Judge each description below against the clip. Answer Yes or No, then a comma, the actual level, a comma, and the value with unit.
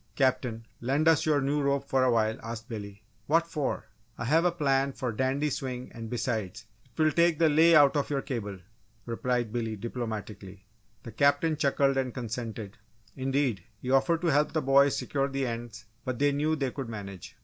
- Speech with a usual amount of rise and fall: Yes, average, 3.8 semitones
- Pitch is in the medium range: No, low, 130 Hz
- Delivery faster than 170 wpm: Yes, average, 195 wpm